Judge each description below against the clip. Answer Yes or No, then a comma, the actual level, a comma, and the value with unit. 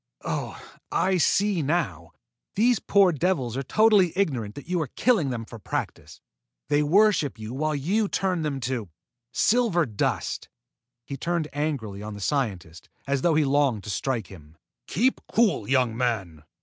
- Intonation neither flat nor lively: No, wide, 7.9 semitones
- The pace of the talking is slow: No, average, 160 wpm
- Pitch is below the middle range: No, medium, 145 Hz